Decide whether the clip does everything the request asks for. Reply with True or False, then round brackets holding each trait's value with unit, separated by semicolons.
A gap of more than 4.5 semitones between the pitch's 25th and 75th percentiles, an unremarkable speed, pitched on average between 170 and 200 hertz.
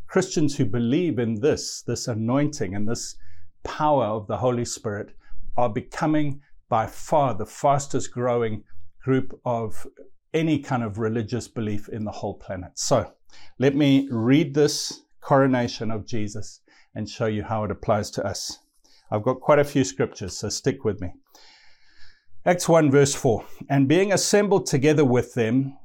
False (5.1 semitones; 160 wpm; 125 Hz)